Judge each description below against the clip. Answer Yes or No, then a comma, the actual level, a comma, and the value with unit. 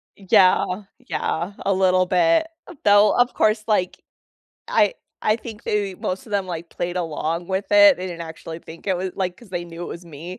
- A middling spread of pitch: Yes, average, 3.0 semitones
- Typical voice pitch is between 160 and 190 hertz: Yes, medium, 185 Hz